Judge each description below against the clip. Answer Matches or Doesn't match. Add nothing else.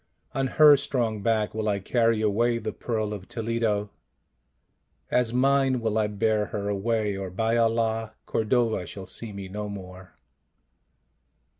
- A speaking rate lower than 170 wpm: Matches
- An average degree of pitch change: Doesn't match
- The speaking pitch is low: Matches